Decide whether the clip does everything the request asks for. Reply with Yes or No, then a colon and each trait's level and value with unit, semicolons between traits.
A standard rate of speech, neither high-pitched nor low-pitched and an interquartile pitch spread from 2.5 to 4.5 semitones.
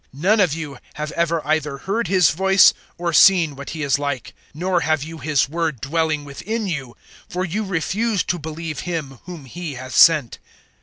Yes: average, 190 wpm; medium, 160 Hz; average, 3.7 semitones